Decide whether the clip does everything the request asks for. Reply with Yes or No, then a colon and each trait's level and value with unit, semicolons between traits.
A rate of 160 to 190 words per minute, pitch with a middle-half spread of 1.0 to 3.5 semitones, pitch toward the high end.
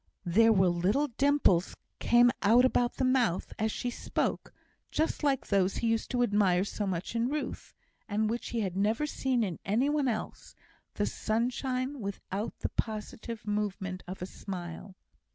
No: average, 165 wpm; average, 4.2 semitones; high, 220 Hz